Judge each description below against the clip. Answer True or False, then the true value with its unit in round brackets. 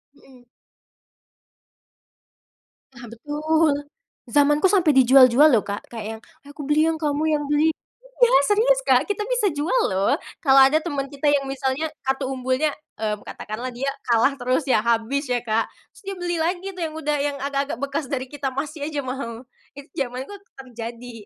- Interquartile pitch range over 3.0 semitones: True (3.4 semitones)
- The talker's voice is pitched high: True (280 Hz)